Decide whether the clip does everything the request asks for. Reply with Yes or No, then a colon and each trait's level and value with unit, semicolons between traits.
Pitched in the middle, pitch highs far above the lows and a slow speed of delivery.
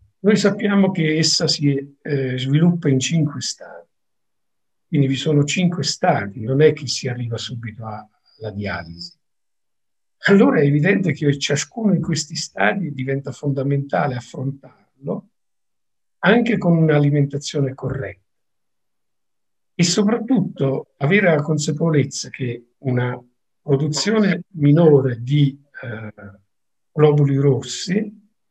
No: medium, 145 Hz; average, 4.1 semitones; slow, 110 wpm